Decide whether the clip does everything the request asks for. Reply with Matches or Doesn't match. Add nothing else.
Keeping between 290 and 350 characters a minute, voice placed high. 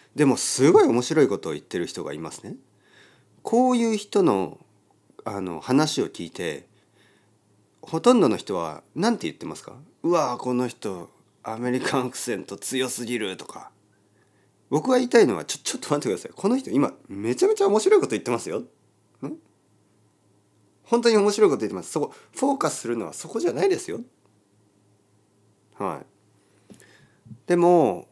Doesn't match